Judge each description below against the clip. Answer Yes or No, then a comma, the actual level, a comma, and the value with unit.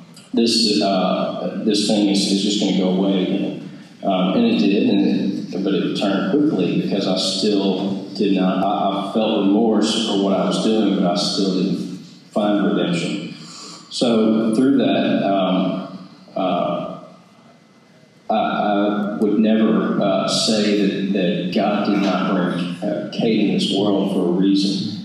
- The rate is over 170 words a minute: No, average, 160 wpm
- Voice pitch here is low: Yes, low, 100 Hz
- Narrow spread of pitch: Yes, narrow, 1.5 semitones